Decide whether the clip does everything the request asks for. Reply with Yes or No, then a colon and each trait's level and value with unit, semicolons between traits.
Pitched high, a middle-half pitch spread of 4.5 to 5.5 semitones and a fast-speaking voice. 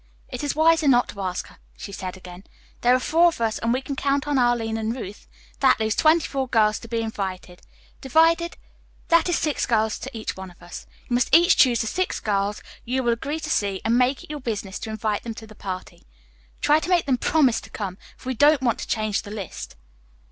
Yes: high, 235 Hz; average, 5.0 semitones; fast, 235 wpm